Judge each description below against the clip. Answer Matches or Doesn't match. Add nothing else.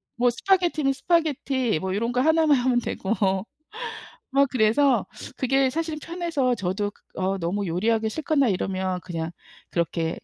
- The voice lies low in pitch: Doesn't match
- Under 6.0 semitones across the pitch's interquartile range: Doesn't match